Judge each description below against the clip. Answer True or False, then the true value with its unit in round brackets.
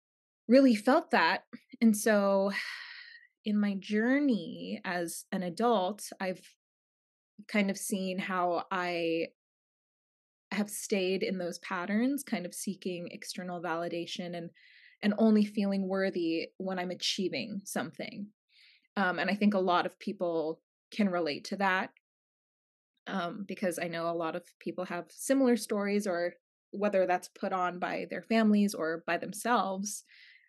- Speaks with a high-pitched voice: True (195 Hz)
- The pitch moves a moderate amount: True (3.7 semitones)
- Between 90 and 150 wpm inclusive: True (140 wpm)